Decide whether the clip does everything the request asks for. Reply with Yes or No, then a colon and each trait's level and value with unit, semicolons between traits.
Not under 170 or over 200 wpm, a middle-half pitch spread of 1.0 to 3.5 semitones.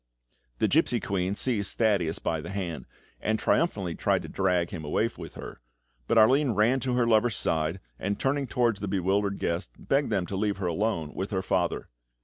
No: average, 190 wpm; average, 4.1 semitones